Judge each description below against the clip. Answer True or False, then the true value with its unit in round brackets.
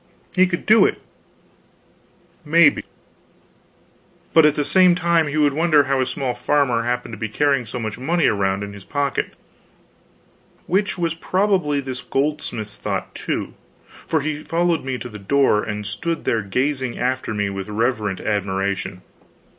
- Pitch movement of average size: False (6.5 semitones)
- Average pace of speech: True (155 wpm)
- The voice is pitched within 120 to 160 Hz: True (135 Hz)